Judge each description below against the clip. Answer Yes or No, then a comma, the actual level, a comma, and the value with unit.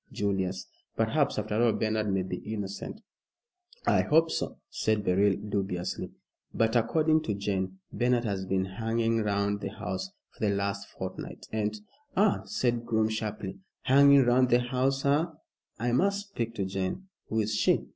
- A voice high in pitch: No, low, 110 Hz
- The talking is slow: No, average, 160 wpm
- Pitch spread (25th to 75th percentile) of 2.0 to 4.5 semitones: Yes, average, 3.8 semitones